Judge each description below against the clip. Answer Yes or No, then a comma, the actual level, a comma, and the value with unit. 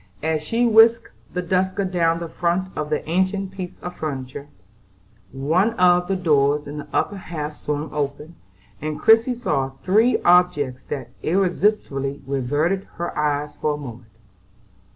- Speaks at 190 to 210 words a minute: No, average, 150 wpm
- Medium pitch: Yes, medium, 165 Hz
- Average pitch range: Yes, average, 4.4 semitones